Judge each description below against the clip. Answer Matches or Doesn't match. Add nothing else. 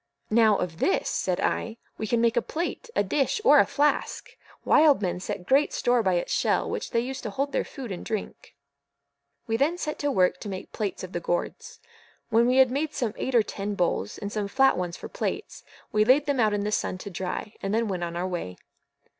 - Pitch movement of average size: Doesn't match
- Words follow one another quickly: Matches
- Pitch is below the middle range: Doesn't match